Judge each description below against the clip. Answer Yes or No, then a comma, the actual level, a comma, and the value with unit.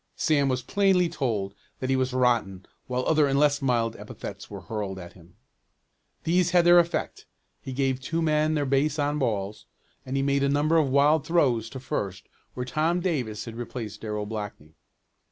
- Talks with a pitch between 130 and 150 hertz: Yes, low, 135 Hz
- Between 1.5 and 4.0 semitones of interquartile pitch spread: No, average, 5.2 semitones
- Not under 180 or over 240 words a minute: Yes, average, 185 wpm